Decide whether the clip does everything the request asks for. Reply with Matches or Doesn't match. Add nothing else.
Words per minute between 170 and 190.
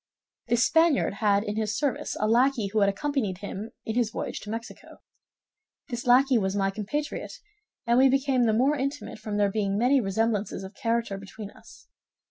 Matches